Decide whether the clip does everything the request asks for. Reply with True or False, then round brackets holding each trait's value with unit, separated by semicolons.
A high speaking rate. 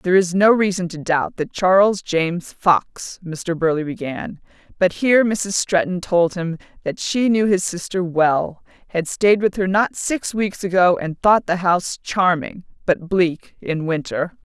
False (175 wpm)